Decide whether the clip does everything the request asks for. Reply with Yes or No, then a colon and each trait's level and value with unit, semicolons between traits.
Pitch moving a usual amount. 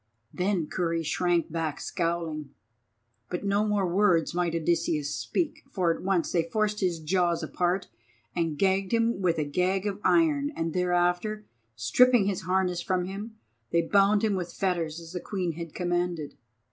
Yes: average, 3.0 semitones